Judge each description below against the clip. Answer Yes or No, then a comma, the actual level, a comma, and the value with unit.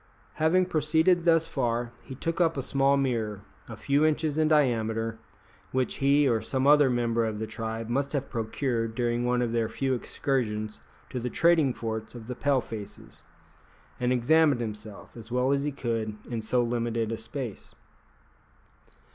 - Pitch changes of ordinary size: Yes, average, 3.8 semitones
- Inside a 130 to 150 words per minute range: No, average, 170 wpm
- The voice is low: Yes, low, 125 Hz